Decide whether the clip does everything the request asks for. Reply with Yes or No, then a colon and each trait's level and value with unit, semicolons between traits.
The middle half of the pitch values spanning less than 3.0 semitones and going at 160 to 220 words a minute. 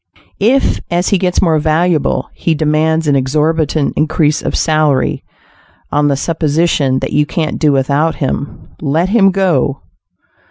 No: narrow, 2.4 semitones; average, 145 wpm